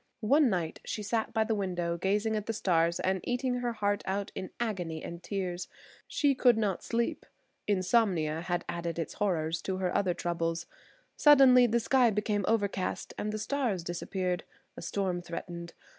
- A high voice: Yes, high, 195 Hz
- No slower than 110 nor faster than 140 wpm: No, average, 170 wpm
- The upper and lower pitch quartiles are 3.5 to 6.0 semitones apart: Yes, average, 4.2 semitones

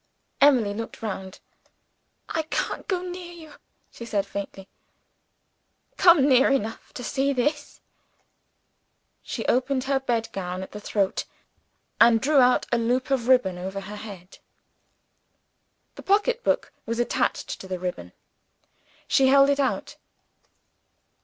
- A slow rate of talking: Yes, slow, 130 wpm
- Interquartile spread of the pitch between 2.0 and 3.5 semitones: No, wide, 5.6 semitones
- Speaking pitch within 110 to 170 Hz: No, high, 245 Hz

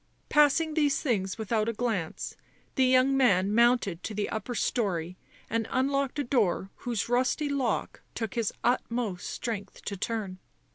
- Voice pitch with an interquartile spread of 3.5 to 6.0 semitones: Yes, average, 4.2 semitones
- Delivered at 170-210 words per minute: No, average, 150 wpm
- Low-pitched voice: No, high, 230 Hz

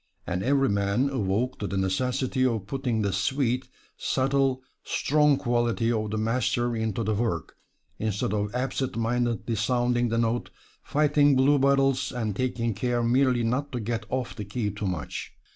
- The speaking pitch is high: No, low, 120 Hz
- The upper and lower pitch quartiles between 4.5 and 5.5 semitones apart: No, average, 3.2 semitones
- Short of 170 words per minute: Yes, average, 160 wpm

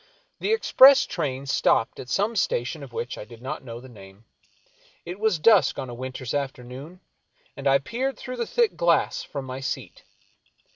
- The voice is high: No, low, 135 Hz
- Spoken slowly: No, average, 180 wpm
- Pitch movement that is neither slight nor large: No, wide, 7.4 semitones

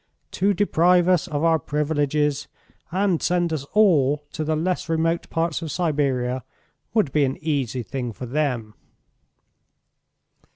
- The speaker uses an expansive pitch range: No, average, 3.7 semitones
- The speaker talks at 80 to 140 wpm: Yes, slow, 135 wpm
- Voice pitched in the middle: Yes, medium, 155 Hz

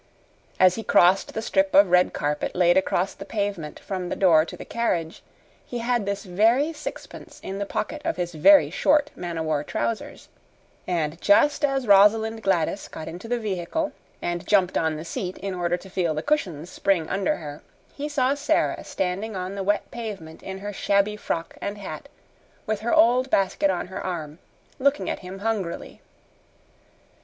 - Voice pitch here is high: Yes, high, 195 Hz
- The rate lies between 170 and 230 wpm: Yes, average, 180 wpm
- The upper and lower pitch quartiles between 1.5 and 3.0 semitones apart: No, average, 4.1 semitones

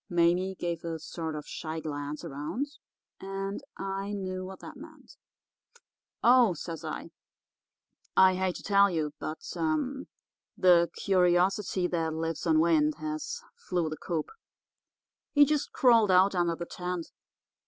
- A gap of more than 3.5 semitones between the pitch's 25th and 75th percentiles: No, average, 3.2 semitones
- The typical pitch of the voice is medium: Yes, medium, 180 Hz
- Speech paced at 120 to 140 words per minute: Yes, slow, 135 wpm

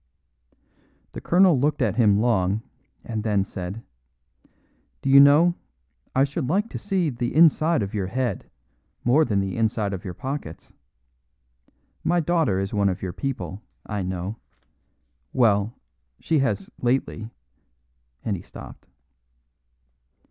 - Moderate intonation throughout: No, wide, 6.4 semitones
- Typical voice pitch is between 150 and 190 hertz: No, low, 115 Hz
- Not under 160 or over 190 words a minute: No, slow, 135 wpm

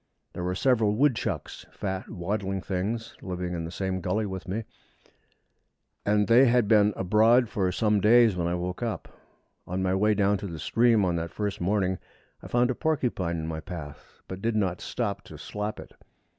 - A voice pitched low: Yes, low, 100 Hz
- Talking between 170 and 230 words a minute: Yes, average, 185 wpm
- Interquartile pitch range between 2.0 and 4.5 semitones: Yes, average, 3.4 semitones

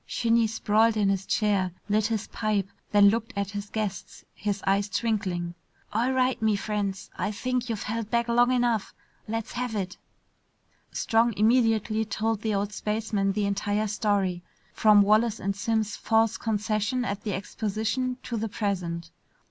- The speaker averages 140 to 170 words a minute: Yes, average, 155 wpm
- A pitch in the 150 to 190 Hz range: No, high, 215 Hz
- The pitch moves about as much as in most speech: No, narrow, 2.1 semitones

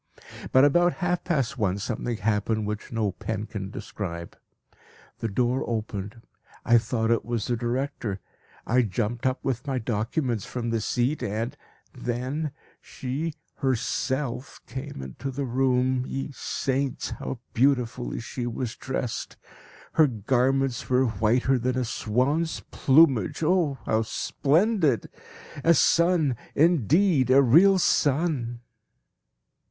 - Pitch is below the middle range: Yes, low, 125 Hz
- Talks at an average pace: No, slow, 125 wpm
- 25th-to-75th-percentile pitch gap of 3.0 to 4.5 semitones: Yes, average, 3.6 semitones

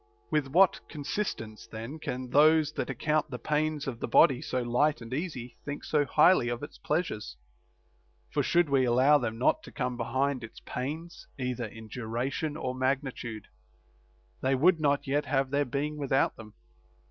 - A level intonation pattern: No, average, 3.6 semitones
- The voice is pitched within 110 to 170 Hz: Yes, low, 135 Hz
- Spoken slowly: No, average, 170 wpm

